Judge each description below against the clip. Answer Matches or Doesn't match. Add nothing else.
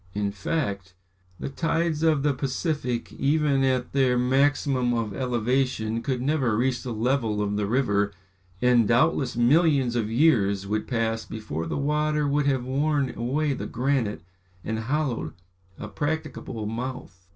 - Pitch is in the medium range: Doesn't match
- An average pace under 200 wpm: Matches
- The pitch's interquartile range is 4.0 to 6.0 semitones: Matches